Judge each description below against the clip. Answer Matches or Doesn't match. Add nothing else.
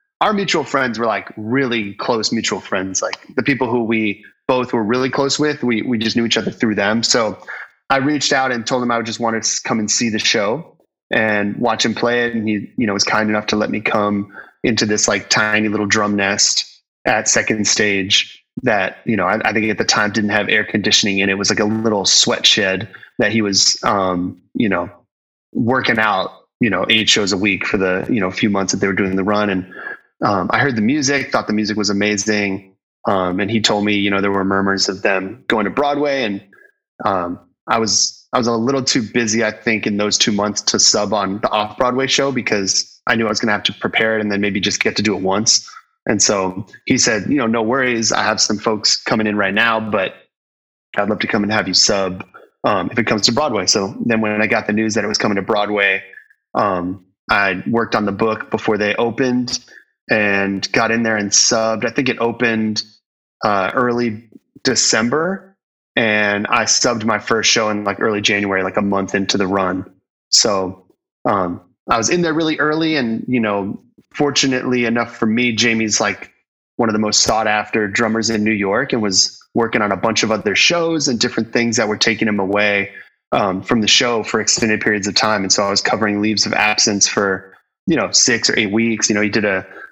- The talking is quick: Matches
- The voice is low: Matches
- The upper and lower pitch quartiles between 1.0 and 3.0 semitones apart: Matches